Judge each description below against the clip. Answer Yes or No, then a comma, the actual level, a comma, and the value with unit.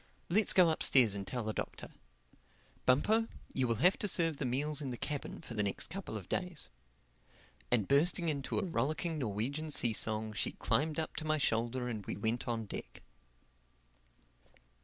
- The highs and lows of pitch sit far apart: Yes, wide, 6.0 semitones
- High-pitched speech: No, low, 135 Hz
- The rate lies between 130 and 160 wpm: No, average, 175 wpm